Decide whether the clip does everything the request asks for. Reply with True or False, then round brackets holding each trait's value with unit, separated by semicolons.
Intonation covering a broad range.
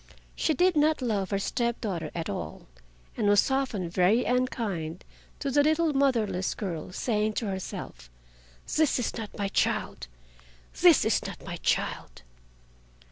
True (6.0 semitones)